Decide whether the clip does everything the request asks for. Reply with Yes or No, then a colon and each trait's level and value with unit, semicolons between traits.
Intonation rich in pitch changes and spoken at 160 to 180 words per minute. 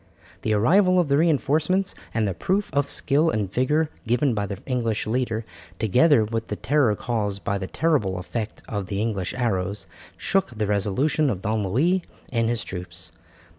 Yes: wide, 6.2 semitones; average, 170 wpm